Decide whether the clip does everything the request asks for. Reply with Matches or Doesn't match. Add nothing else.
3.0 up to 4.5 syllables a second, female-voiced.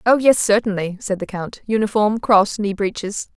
Doesn't match